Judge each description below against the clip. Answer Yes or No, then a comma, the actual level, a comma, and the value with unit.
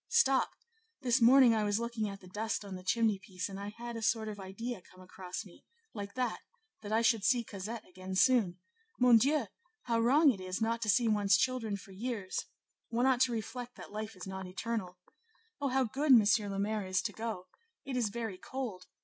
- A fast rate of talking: Yes, fast, 210 wpm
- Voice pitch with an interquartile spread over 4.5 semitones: No, average, 3.6 semitones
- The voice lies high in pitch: Yes, high, 220 Hz